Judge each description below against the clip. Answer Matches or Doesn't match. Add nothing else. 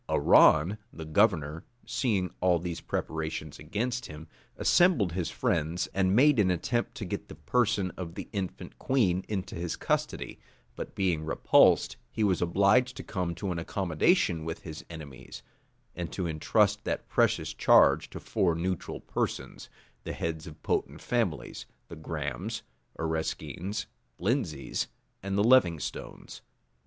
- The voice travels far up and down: Doesn't match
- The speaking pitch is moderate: Doesn't match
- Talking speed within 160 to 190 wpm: Doesn't match